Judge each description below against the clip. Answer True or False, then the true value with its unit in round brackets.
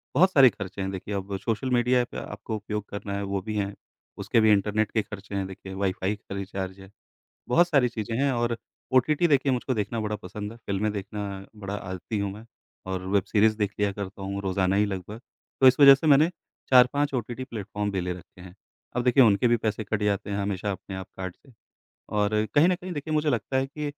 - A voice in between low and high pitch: False (105 Hz)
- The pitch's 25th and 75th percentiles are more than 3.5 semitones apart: True (3.9 semitones)